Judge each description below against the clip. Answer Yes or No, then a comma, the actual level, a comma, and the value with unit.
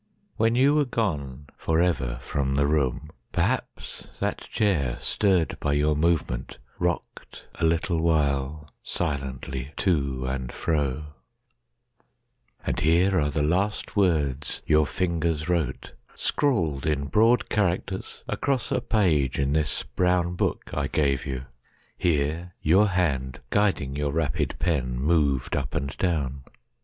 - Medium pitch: No, very low, 75 Hz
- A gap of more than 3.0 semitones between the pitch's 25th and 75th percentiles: Yes, average, 4.4 semitones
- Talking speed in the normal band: No, slow, 110 wpm